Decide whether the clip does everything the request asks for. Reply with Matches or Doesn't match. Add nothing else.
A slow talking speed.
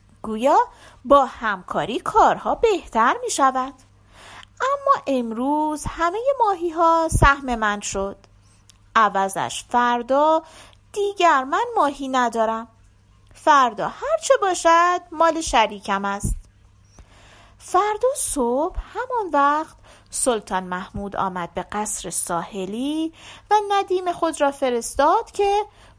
Matches